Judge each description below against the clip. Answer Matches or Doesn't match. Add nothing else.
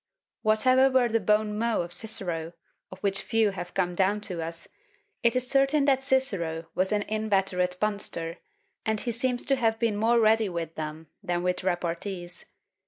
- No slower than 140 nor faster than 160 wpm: Doesn't match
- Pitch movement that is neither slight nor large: Matches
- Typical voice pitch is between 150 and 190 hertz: Doesn't match